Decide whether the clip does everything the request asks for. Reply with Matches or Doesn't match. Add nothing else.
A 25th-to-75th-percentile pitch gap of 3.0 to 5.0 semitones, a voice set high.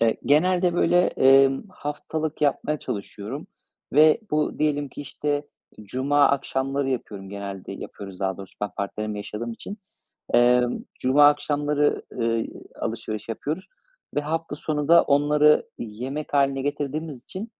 Doesn't match